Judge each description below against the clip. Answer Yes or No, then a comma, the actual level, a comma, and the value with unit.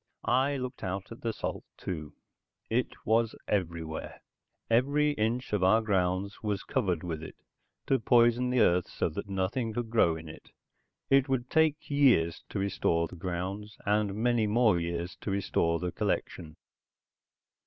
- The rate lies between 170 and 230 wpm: No, average, 155 wpm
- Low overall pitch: Yes, low, 105 Hz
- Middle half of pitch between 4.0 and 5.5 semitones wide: Yes, average, 5.2 semitones